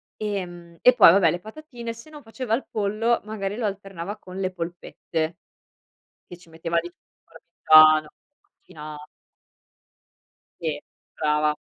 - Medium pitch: Yes, medium, 180 Hz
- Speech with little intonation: No, average, 4.9 semitones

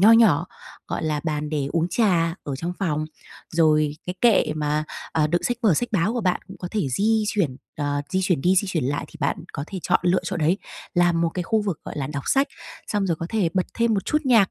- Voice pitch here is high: No, medium, 175 Hz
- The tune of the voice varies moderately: Yes, average, 4.9 semitones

